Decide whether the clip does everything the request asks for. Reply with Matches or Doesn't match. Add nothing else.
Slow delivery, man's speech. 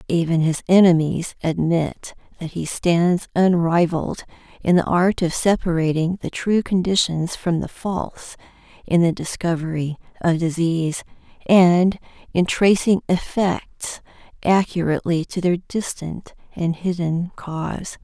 Doesn't match